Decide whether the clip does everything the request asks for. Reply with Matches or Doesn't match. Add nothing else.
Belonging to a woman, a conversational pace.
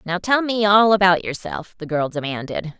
Matches